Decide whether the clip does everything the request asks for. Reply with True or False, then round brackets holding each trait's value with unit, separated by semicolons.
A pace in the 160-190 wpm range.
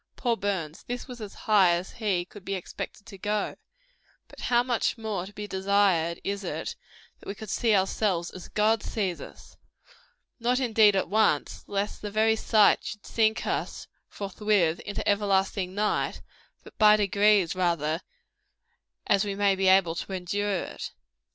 True (165 wpm)